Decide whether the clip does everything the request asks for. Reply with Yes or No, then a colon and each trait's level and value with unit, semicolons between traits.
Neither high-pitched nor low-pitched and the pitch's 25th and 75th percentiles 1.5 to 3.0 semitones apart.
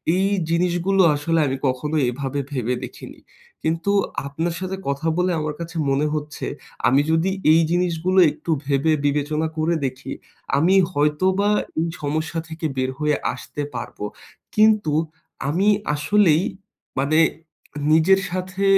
No: medium, 160 Hz; average, 3.8 semitones